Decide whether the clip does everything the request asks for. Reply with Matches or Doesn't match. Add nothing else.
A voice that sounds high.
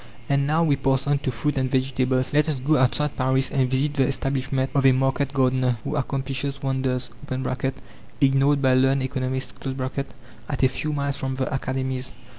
Doesn't match